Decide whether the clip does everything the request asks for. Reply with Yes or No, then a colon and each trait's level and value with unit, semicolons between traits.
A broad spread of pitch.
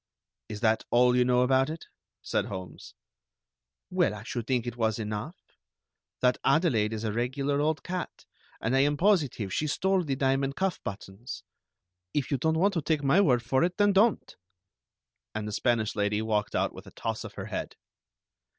Yes: wide, 5.8 semitones